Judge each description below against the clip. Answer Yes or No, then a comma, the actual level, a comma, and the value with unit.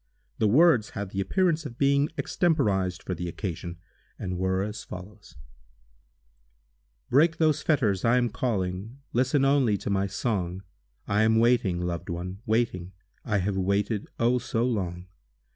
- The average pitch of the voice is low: Yes, low, 105 Hz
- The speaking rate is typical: No, slow, 130 wpm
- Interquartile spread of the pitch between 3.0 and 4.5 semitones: No, average, 5.0 semitones